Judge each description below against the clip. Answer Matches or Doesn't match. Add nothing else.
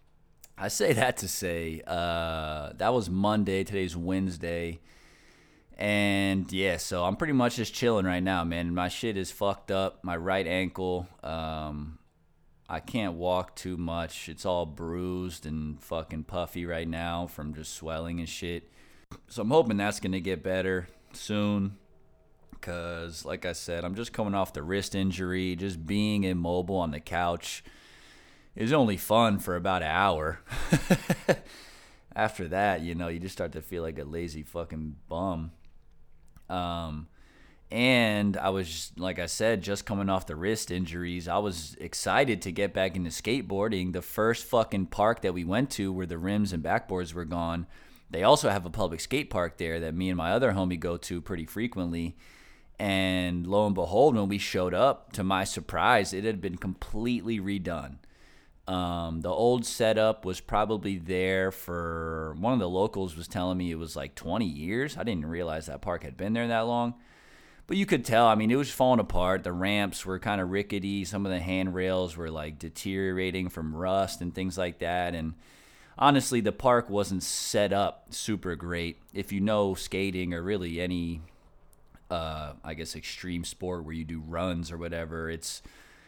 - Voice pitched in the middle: Doesn't match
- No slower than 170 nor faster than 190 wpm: Matches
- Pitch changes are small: Doesn't match